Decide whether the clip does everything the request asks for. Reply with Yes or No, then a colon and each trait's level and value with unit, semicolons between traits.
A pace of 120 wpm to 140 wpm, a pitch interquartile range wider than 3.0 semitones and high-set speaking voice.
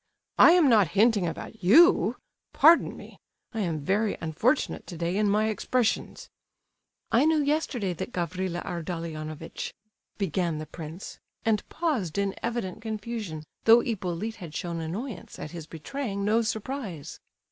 Yes: slow, 135 wpm; wide, 5.4 semitones; high, 200 Hz